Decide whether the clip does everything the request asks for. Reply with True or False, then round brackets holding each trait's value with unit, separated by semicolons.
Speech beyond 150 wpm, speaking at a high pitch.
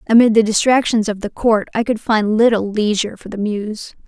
True (205 wpm; 215 Hz)